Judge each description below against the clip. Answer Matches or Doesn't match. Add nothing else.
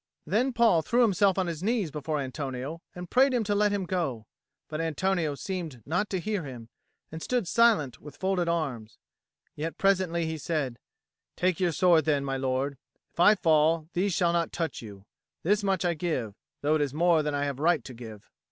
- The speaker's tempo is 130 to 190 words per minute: Doesn't match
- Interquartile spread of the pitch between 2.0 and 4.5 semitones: Doesn't match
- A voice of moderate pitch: Matches